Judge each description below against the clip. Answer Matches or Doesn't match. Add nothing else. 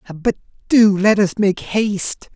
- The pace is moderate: Matches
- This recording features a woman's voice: Doesn't match